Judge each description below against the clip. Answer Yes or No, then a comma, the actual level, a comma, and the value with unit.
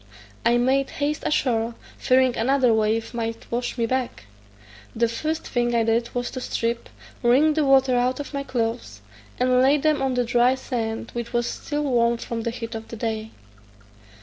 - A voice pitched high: Yes, high, 240 Hz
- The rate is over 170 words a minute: Yes, average, 180 wpm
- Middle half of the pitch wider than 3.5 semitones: No, narrow, 2.4 semitones